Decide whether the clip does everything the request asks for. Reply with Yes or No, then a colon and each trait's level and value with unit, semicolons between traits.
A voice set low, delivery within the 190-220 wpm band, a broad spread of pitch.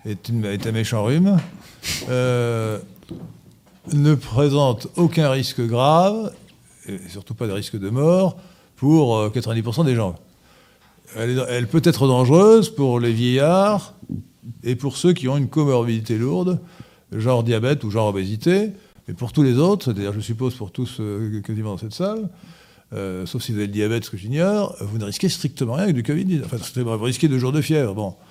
No: low, 125 Hz; average, 180 wpm; wide, 6.4 semitones